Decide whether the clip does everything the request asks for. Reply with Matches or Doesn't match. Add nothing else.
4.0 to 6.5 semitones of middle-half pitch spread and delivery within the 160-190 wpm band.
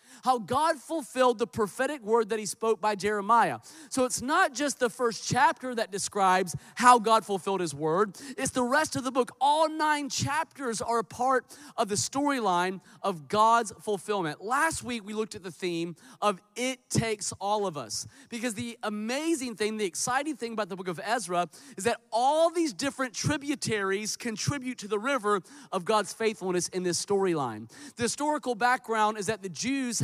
Matches